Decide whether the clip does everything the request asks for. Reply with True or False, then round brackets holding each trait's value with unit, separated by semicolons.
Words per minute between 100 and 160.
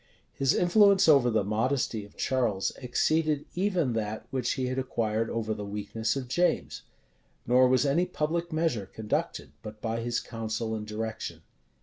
True (155 wpm)